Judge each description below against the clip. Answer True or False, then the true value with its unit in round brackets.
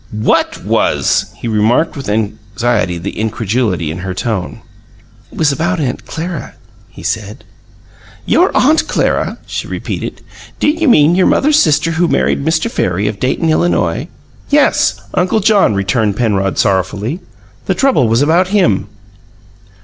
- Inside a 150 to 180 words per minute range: False (140 wpm)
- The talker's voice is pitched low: True (120 Hz)